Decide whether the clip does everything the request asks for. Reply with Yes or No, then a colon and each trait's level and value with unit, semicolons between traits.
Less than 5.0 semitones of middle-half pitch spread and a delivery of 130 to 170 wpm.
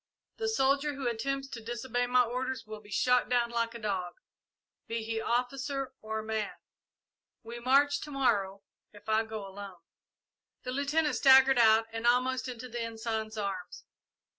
Yes: average, 3.1 semitones; average, 160 wpm